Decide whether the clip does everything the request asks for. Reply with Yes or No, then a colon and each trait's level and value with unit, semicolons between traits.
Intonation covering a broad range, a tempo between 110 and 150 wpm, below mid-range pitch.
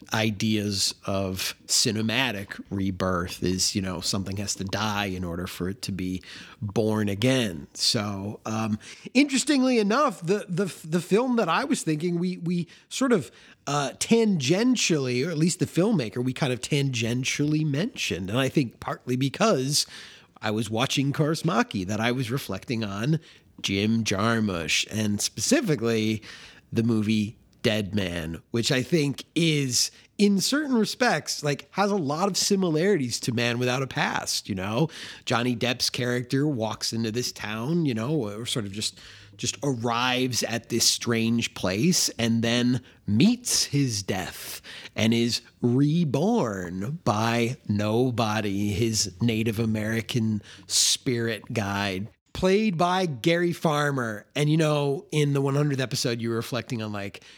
Yes: wide, 6.1 semitones; average, 145 wpm; low, 120 Hz